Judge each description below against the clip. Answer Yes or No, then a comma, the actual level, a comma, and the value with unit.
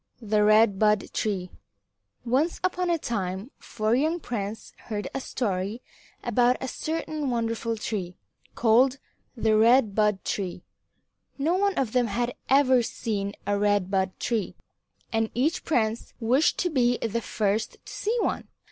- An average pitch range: Yes, average, 3.8 semitones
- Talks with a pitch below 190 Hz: No, high, 230 Hz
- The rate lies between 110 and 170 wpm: Yes, average, 150 wpm